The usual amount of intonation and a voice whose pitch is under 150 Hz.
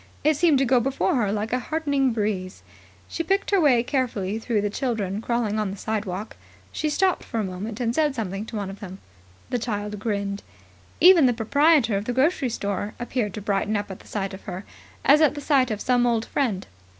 No: average, 4.8 semitones; high, 225 Hz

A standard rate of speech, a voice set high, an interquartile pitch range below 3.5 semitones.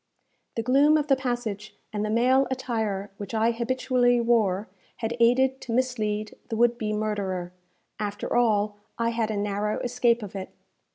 Yes: average, 165 wpm; high, 230 Hz; average, 2.7 semitones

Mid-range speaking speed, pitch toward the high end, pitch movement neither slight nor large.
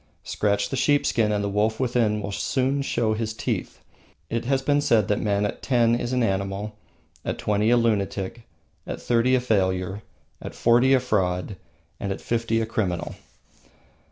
No: average, 180 wpm; low, 110 Hz; average, 3.1 semitones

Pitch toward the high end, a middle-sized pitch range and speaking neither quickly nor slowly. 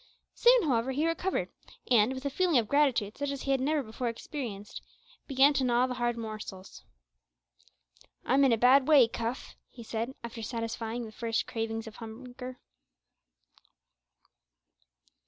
Yes: high, 245 Hz; average, 3.3 semitones; average, 150 wpm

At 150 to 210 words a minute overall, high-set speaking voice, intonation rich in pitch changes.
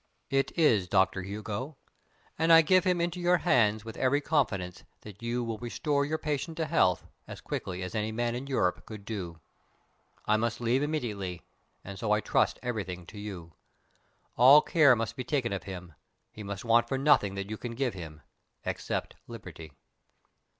No: average, 180 wpm; low, 115 Hz; wide, 6.0 semitones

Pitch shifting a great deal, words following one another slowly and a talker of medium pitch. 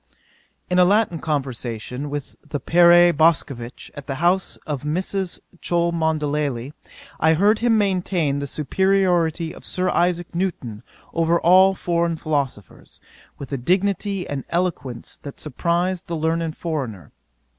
No: average, 4.0 semitones; slow, 130 wpm; medium, 165 Hz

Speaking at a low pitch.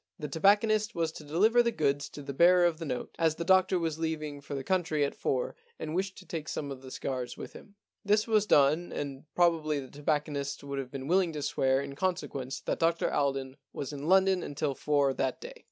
No: medium, 155 Hz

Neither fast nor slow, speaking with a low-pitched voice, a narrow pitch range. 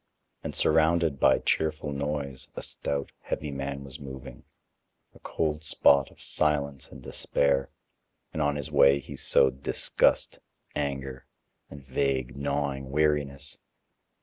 No: slow, 125 wpm; very low, 70 Hz; narrow, 1.5 semitones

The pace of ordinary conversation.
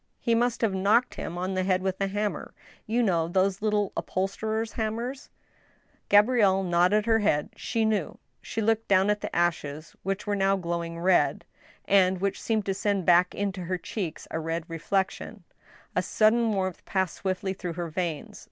Yes: average, 180 wpm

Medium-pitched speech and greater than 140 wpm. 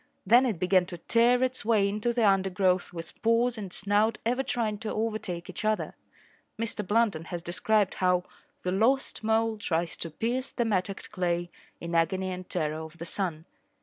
No: high, 200 Hz; average, 180 wpm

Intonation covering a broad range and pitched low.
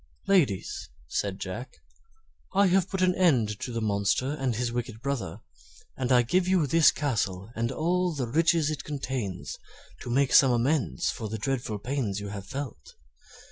Yes: wide, 5.9 semitones; low, 130 Hz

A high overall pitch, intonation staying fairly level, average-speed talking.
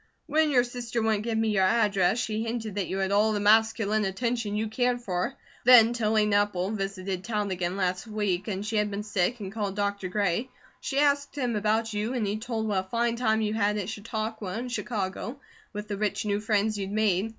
No: high, 215 Hz; narrow, 2.3 semitones; fast, 215 wpm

